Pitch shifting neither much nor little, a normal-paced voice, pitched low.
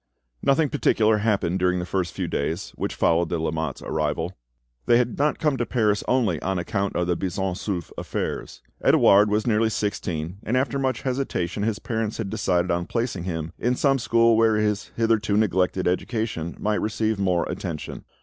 Yes: average, 4.4 semitones; average, 180 wpm; low, 105 Hz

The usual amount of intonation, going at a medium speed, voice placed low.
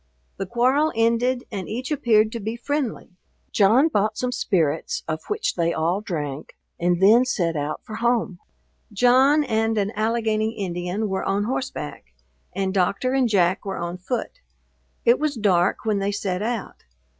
No: average, 4.7 semitones; average, 160 wpm; high, 215 Hz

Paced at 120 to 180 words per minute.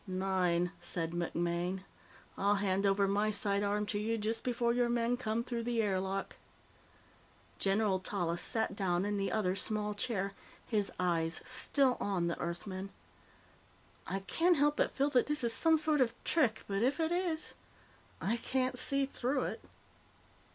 Yes: average, 160 wpm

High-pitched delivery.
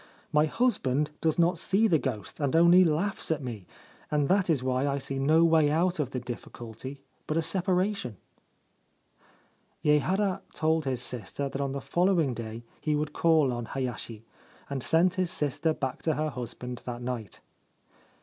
No: medium, 150 Hz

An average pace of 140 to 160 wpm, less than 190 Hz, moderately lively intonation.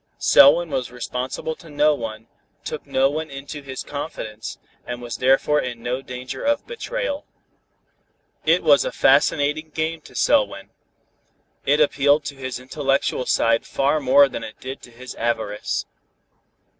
Yes: average, 145 wpm; low, 135 Hz; average, 3.5 semitones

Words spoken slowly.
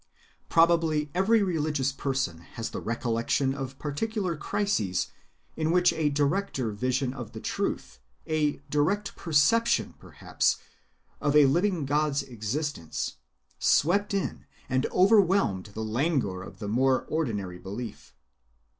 Yes: slow, 120 wpm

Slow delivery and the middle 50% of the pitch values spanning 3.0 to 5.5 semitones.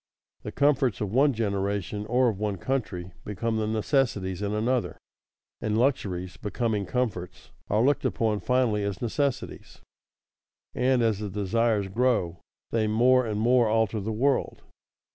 No: average, 145 wpm; average, 3.5 semitones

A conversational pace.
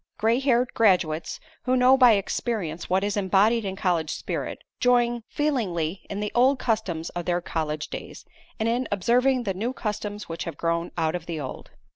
Yes: average, 180 wpm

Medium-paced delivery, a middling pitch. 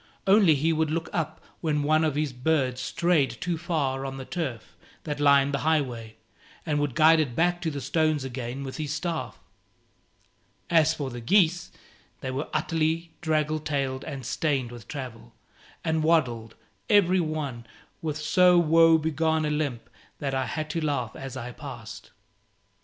Yes: average, 165 wpm; medium, 150 Hz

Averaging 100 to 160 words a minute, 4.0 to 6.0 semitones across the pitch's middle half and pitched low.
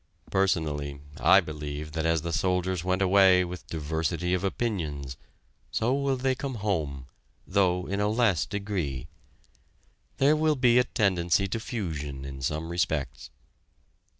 Yes: average, 140 wpm; average, 5.2 semitones; very low, 90 Hz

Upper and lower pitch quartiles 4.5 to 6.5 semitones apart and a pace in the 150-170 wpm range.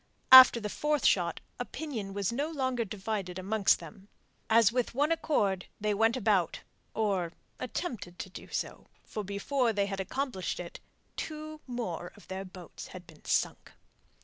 Yes: average, 5.1 semitones; average, 155 wpm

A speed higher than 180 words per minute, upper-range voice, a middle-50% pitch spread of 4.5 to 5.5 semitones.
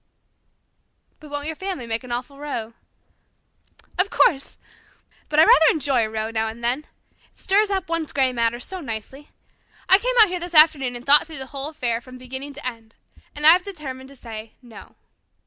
Yes: average, 200 wpm; very high, 275 Hz; average, 4.8 semitones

